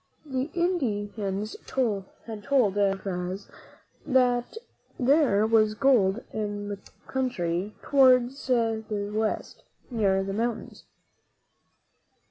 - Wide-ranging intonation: No, average, 4.0 semitones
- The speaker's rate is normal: No, slow, 95 wpm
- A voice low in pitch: No, high, 220 Hz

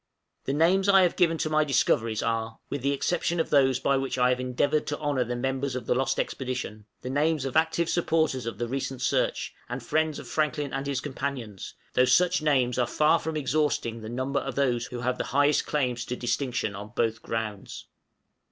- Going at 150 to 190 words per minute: No, fast, 205 wpm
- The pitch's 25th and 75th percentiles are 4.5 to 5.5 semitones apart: No, average, 3.7 semitones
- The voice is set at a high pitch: No, low, 135 Hz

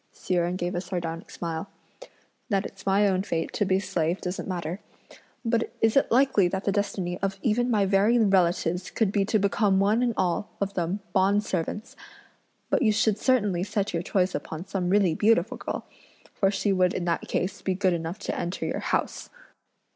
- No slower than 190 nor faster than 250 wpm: Yes, average, 195 wpm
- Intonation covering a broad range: No, average, 2.8 semitones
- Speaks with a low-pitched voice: No, high, 195 Hz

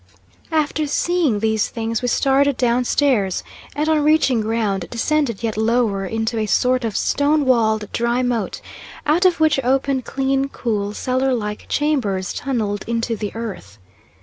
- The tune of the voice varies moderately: Yes, average, 4.1 semitones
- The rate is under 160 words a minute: Yes, average, 150 wpm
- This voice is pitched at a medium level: No, high, 240 Hz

